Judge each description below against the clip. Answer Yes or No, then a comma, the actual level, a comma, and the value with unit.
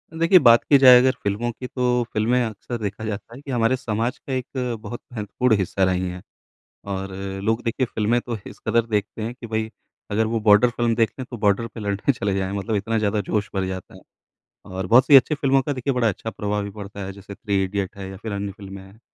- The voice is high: No, low, 110 Hz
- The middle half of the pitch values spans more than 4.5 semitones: No, average, 3.4 semitones